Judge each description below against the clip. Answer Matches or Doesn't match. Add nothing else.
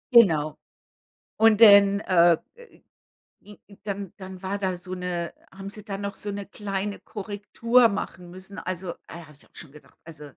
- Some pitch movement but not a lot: Doesn't match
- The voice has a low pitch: Doesn't match